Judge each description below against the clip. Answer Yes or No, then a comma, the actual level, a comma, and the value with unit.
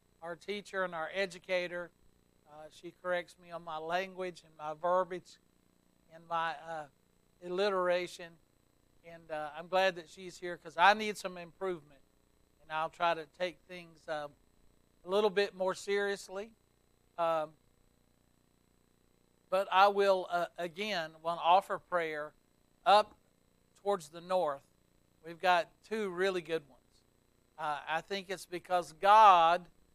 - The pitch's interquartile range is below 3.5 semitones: No, average, 4.0 semitones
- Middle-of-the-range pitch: Yes, medium, 170 Hz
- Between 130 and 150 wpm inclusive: Yes, average, 140 wpm